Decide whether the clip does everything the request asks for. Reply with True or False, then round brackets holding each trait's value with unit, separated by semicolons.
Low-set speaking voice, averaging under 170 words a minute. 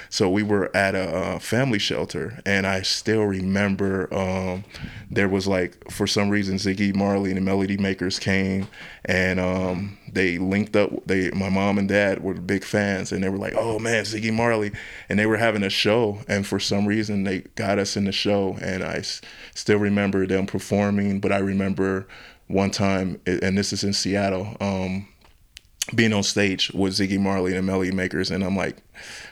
False (95 Hz; 190 wpm)